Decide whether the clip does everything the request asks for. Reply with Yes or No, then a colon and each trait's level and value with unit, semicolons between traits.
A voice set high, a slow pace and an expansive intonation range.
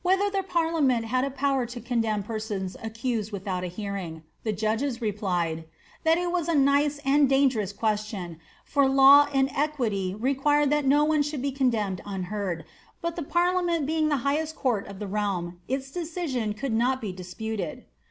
No: very high, 255 Hz; average, 165 wpm; wide, 5.9 semitones